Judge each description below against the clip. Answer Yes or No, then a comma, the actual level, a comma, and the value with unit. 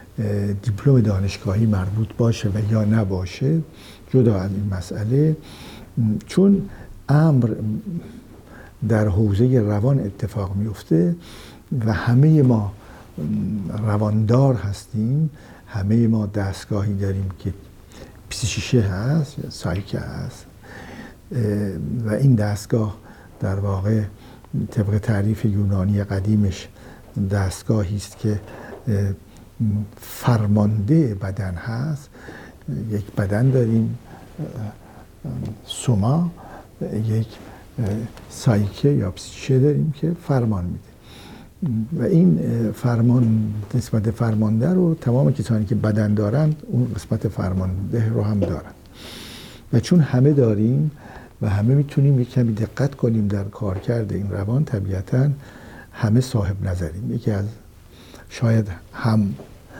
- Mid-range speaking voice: No, low, 110 Hz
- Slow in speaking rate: Yes, slow, 100 wpm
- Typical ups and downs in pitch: Yes, average, 3.4 semitones